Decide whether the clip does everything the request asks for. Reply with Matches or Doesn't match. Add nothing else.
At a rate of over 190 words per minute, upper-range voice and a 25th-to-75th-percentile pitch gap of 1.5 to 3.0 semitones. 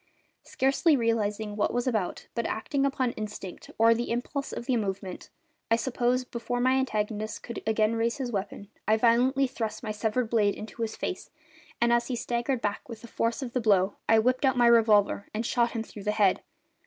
Matches